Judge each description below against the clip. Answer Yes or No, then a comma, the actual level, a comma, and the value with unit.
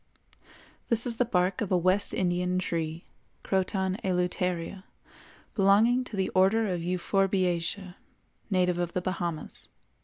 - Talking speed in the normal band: No, slow, 125 wpm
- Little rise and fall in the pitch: Yes, narrow, 1.8 semitones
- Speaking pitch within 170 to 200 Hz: Yes, medium, 185 Hz